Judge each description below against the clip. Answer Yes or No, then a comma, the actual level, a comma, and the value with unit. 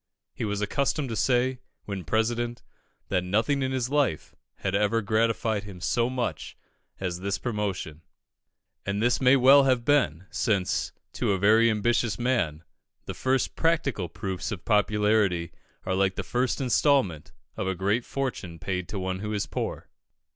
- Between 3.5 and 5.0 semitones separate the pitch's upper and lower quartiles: Yes, average, 4.6 semitones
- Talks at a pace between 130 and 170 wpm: Yes, average, 160 wpm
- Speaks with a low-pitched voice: Yes, low, 105 Hz